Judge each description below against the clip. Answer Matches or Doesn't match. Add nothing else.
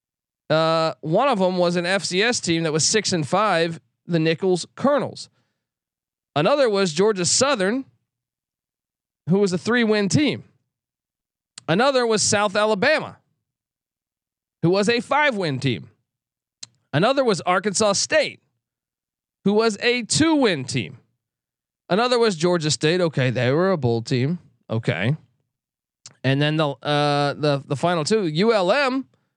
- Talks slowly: Matches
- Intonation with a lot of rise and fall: Matches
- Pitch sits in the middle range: Matches